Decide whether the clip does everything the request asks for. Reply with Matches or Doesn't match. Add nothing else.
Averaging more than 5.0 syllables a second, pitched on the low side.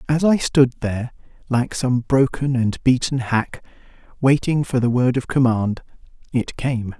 Doesn't match